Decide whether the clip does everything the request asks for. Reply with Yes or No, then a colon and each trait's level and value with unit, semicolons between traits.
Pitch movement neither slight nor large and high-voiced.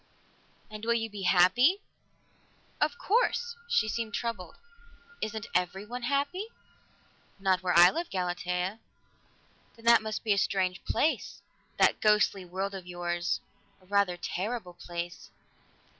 Yes: average, 4.5 semitones; high, 200 Hz